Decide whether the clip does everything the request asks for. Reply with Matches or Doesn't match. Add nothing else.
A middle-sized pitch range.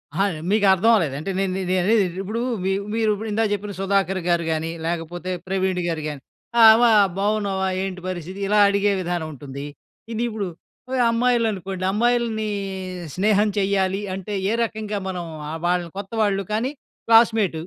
Matches